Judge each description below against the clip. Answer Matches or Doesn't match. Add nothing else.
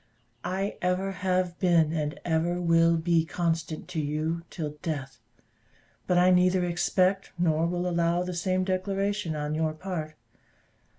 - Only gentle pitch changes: Matches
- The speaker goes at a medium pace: Matches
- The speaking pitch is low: Doesn't match